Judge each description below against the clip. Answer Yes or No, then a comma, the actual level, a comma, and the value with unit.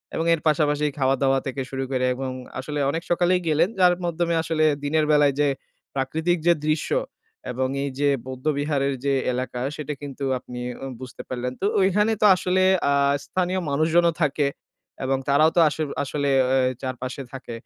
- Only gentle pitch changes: No, average, 3.5 semitones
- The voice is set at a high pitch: No, medium, 145 Hz